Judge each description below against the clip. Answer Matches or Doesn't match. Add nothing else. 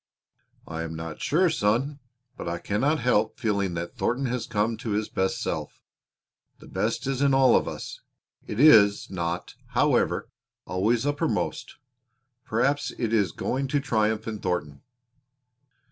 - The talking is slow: Doesn't match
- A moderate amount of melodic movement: Doesn't match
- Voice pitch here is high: Doesn't match